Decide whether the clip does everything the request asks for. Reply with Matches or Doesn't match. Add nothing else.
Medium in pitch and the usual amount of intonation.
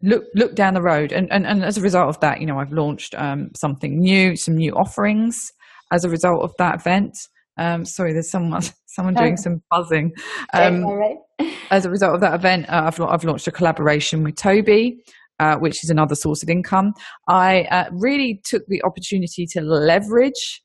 Matches